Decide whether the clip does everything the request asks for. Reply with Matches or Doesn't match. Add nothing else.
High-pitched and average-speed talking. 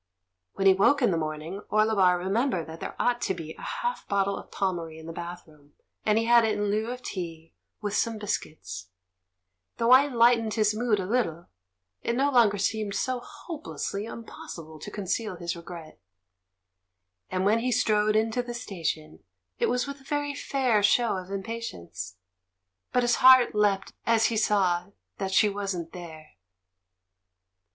Matches